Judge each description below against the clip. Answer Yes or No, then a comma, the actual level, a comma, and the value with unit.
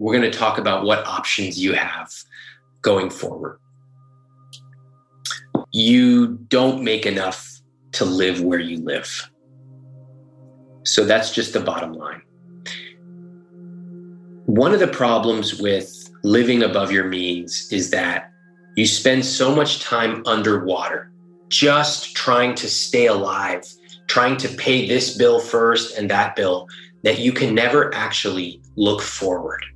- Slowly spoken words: Yes, slow, 130 wpm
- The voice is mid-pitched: No, low, 130 Hz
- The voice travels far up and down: No, average, 4.1 semitones